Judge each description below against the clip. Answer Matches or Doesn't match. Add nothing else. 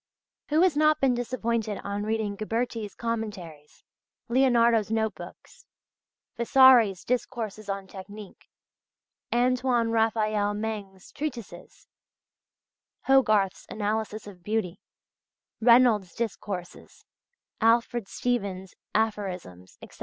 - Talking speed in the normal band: Doesn't match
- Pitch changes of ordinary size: Matches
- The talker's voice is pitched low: Doesn't match